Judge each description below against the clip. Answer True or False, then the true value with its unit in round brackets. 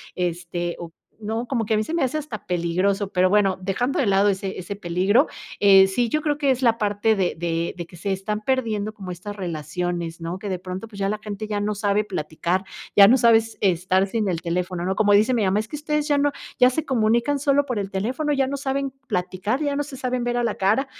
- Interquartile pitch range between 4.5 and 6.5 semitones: True (5.0 semitones)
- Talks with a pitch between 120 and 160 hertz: False (205 Hz)